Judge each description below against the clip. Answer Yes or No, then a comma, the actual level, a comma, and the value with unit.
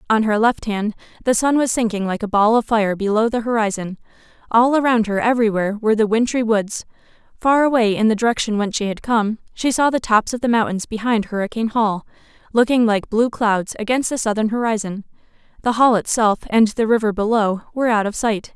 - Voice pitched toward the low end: No, high, 220 Hz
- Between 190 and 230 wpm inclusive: Yes, average, 200 wpm